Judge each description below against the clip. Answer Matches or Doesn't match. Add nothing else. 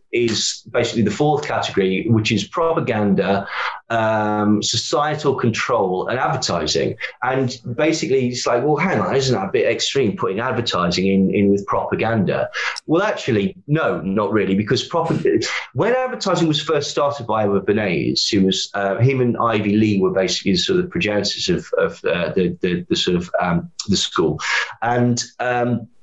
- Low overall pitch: Matches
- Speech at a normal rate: Matches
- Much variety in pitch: Matches